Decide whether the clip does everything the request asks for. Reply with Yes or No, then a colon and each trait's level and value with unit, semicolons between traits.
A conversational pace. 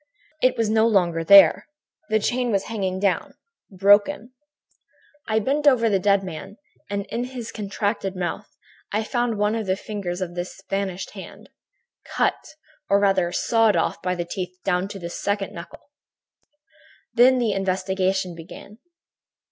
Yes: average, 150 wpm